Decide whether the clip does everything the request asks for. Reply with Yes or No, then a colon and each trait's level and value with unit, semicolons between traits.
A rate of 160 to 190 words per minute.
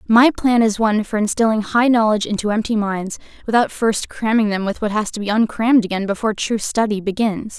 No: fast, 205 wpm